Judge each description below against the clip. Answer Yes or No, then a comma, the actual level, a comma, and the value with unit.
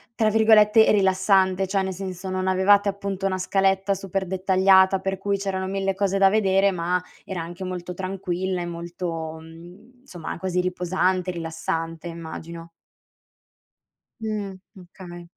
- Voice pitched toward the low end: No, high, 190 Hz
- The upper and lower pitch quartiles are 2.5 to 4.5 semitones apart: No, narrow, 1.8 semitones